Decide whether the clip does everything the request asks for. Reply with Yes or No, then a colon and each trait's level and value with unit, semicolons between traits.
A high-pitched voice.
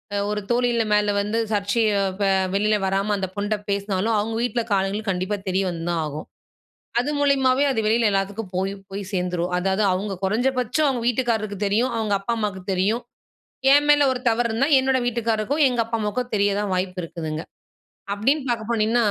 Yes: high, 215 Hz